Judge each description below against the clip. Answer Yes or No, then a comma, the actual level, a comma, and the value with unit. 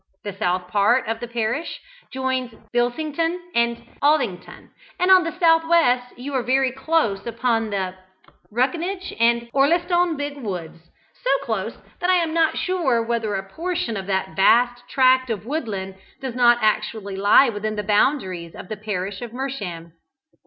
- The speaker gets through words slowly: No, average, 160 wpm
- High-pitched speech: Yes, high, 240 Hz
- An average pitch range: No, wide, 5.9 semitones